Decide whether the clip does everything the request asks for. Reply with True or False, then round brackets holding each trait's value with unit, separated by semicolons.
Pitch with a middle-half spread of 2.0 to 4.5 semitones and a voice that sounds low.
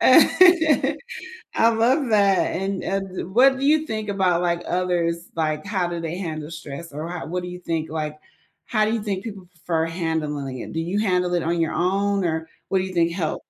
False (3.6 semitones; 180 Hz)